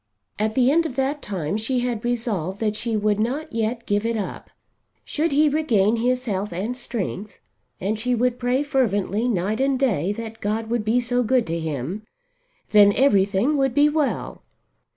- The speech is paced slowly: No, average, 180 wpm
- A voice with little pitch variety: No, average, 3.8 semitones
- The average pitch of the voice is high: Yes, high, 230 Hz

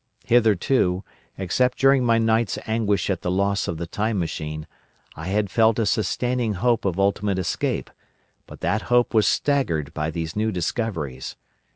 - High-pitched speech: No, low, 105 Hz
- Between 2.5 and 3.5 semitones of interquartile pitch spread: No, average, 4.4 semitones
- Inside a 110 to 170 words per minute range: Yes, average, 160 wpm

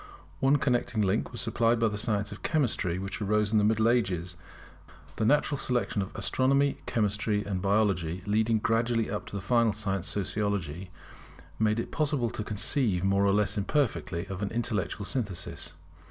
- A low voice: Yes, low, 105 Hz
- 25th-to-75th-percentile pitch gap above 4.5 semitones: No, average, 3.0 semitones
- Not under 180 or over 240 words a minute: No, average, 170 wpm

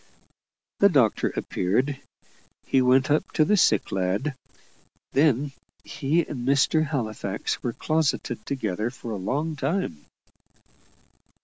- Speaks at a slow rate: Yes, slow, 115 wpm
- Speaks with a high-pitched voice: No, low, 135 Hz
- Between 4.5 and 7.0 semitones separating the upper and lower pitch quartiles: Yes, wide, 5.6 semitones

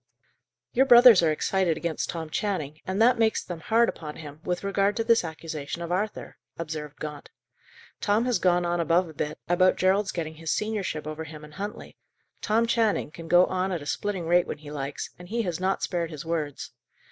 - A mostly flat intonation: No, average, 4.5 semitones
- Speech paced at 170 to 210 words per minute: Yes, fast, 205 wpm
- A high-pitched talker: No, medium, 175 Hz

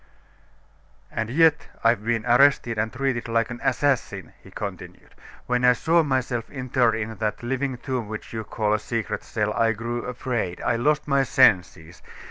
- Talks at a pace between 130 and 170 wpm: Yes, average, 165 wpm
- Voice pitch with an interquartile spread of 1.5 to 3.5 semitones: Yes, average, 2.8 semitones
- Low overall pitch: Yes, low, 120 Hz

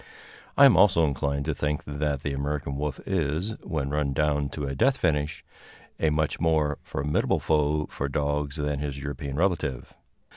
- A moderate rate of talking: Yes, average, 170 wpm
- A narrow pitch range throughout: Yes, narrow, 1.7 semitones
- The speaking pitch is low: Yes, very low, 75 Hz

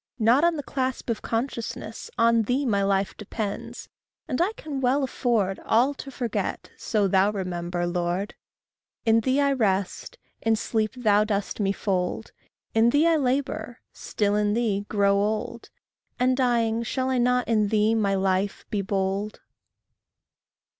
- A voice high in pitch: Yes, high, 220 Hz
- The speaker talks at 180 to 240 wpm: No, average, 155 wpm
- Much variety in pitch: No, average, 3.9 semitones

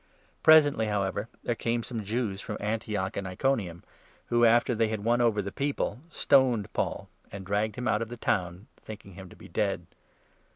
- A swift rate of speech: No, average, 190 wpm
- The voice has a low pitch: Yes, low, 110 Hz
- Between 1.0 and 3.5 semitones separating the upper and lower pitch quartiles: Yes, average, 3.2 semitones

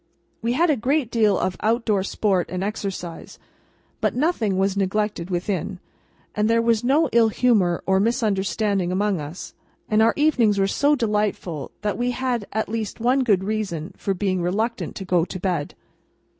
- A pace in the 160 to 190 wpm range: Yes, average, 170 wpm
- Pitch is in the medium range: No, high, 210 Hz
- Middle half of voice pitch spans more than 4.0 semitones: No, average, 3.6 semitones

